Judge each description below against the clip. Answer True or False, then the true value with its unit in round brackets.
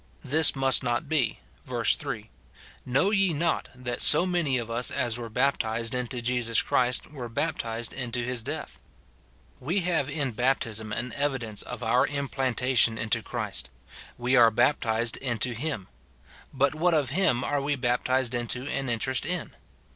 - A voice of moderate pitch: False (125 Hz)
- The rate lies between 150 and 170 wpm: True (160 wpm)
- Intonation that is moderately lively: True (3.1 semitones)